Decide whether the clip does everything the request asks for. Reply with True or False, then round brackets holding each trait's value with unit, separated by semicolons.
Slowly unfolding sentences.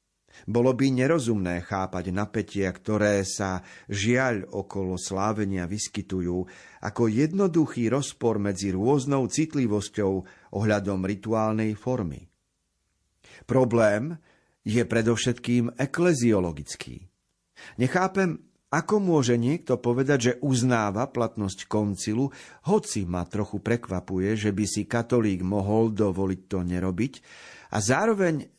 True (100 wpm)